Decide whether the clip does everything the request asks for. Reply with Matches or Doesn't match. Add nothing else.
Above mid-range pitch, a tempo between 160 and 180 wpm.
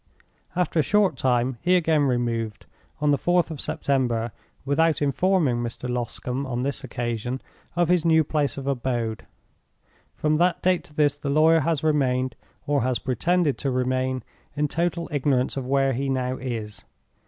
Doesn't match